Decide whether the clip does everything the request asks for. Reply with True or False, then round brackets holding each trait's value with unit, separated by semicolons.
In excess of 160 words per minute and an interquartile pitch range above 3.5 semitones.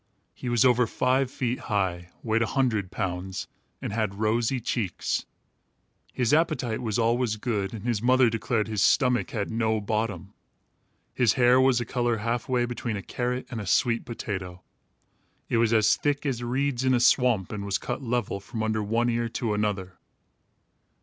False (175 wpm; 2.9 semitones)